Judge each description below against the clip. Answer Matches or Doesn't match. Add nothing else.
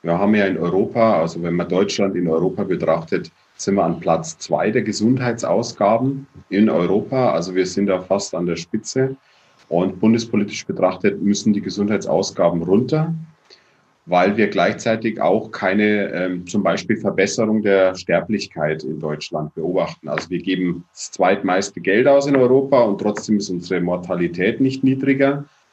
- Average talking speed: Matches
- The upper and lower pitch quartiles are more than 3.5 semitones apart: Matches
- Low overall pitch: Matches